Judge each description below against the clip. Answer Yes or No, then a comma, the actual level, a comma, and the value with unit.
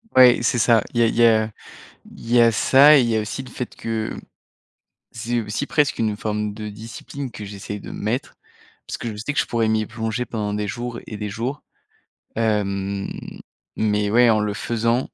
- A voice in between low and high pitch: No, low, 110 Hz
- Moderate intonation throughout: No, narrow, 2.2 semitones